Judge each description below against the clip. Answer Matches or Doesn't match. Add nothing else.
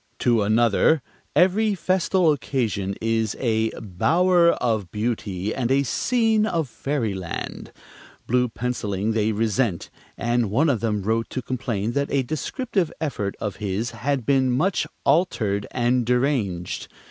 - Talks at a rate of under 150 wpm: Matches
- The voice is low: Matches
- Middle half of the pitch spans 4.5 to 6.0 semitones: Matches